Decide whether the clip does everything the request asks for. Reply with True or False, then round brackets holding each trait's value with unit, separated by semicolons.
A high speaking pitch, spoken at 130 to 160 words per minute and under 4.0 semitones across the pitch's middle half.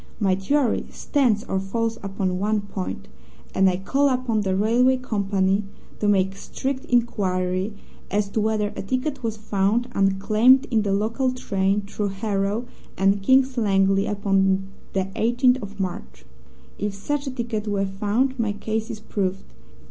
True (205 Hz; 155 wpm; 3.4 semitones)